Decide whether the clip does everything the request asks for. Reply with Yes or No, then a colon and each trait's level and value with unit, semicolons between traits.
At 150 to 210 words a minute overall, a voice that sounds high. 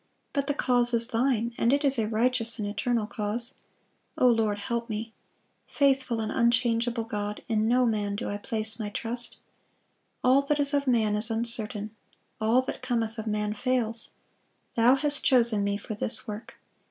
Yes: average, 175 wpm; high, 230 Hz